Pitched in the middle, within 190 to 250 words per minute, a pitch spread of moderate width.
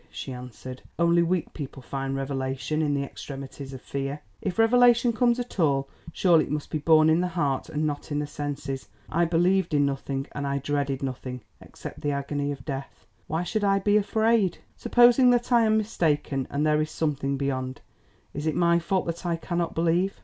Yes: medium, 150 Hz; average, 195 wpm; average, 4.5 semitones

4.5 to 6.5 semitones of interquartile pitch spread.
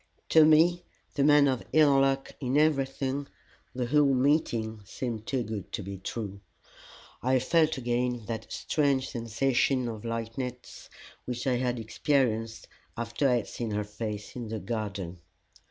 No: average, 3.4 semitones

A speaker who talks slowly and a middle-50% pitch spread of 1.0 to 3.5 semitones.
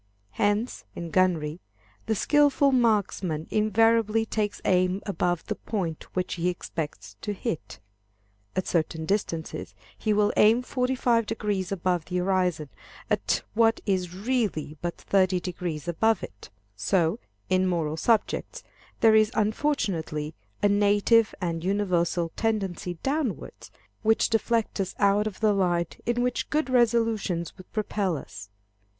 No: slow, 130 wpm; average, 4.3 semitones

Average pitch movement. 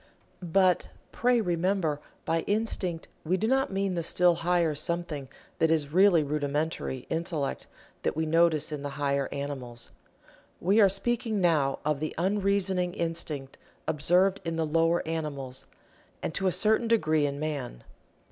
Yes: average, 4.1 semitones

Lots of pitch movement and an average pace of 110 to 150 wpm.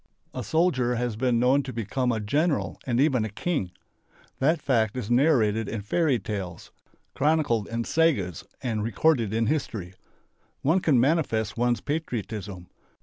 No: average, 5.0 semitones; average, 145 wpm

